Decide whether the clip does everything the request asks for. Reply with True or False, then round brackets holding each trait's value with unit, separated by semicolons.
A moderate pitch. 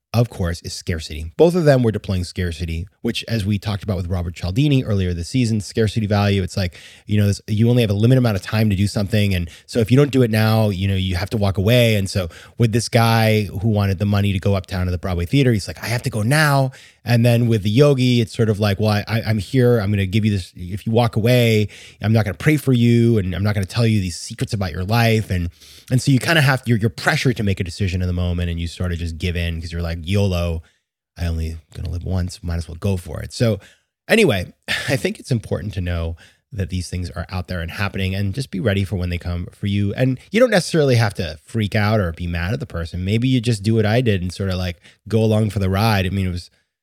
False (105 Hz)